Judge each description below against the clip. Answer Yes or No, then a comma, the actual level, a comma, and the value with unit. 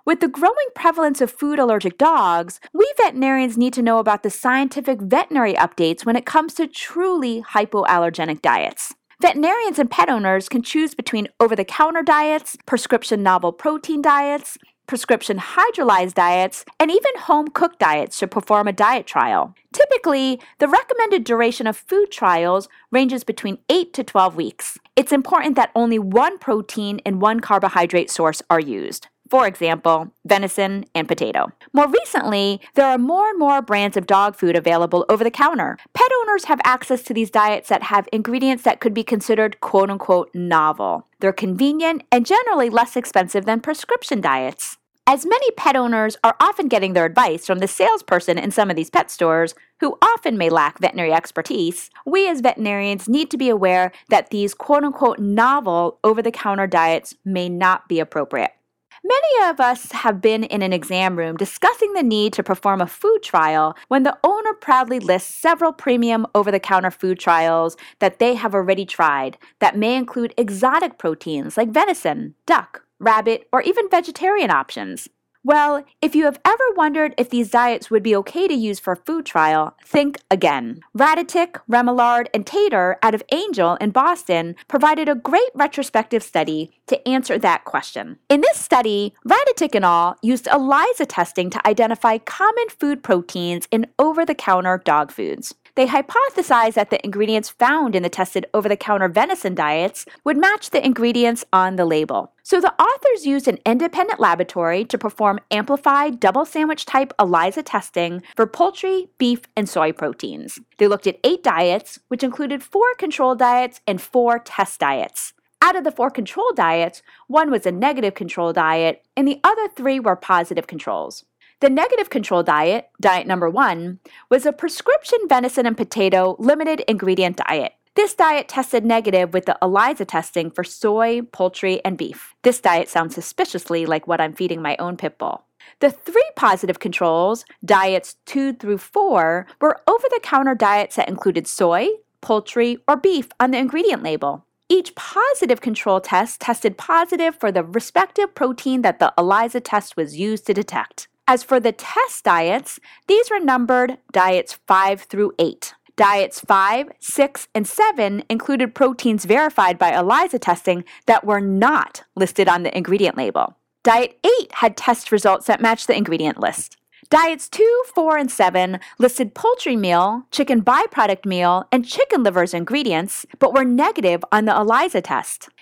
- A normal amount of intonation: No, wide, 7.2 semitones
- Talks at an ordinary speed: Yes, average, 170 wpm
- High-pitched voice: Yes, high, 235 Hz